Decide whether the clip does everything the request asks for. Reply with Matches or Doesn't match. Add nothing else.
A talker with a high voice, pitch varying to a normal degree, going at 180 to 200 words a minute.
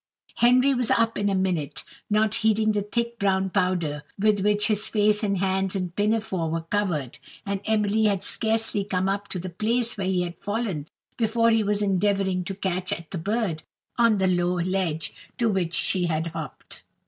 Matches